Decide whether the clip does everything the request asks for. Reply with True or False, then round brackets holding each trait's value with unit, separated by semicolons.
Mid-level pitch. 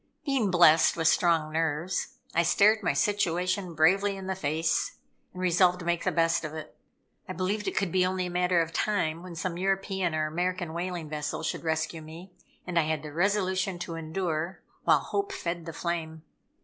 True (175 Hz)